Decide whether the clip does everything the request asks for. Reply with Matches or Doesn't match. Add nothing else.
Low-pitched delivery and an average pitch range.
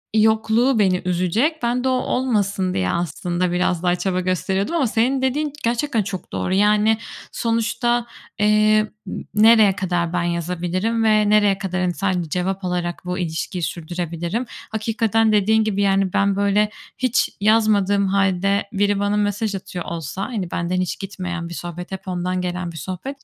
Doesn't match